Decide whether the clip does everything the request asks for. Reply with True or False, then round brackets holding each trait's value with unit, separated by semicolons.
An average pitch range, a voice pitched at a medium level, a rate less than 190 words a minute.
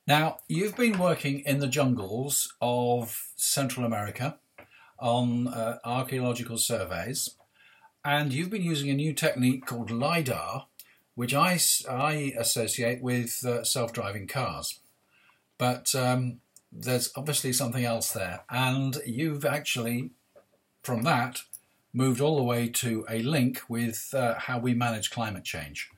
False (3.3 semitones; 125 Hz; 135 wpm)